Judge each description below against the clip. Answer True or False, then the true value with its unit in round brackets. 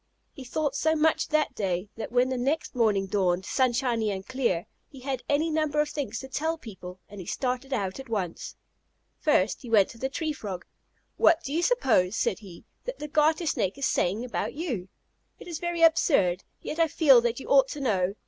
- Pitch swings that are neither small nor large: False (6.9 semitones)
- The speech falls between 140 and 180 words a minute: False (205 wpm)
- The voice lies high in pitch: True (255 Hz)